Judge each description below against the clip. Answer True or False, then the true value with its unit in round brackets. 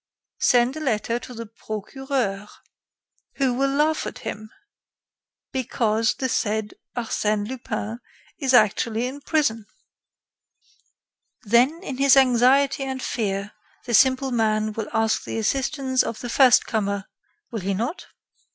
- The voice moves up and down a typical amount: True (3.6 semitones)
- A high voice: True (240 Hz)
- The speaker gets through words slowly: True (130 wpm)